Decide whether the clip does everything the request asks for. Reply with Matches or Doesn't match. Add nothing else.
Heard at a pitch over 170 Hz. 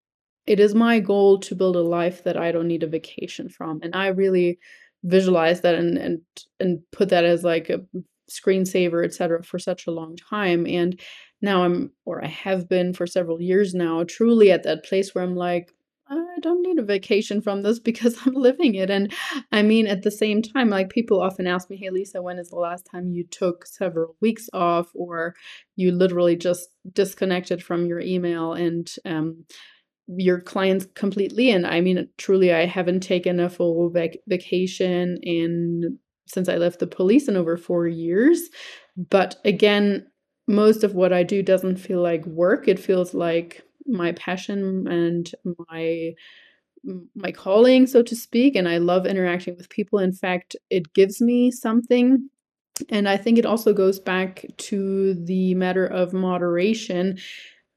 Matches